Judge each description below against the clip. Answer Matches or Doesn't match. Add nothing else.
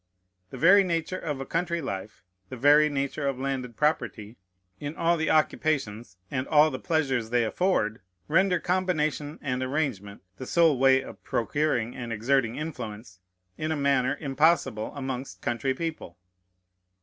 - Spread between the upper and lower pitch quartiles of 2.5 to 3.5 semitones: Doesn't match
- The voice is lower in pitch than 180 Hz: Matches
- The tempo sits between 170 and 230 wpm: Doesn't match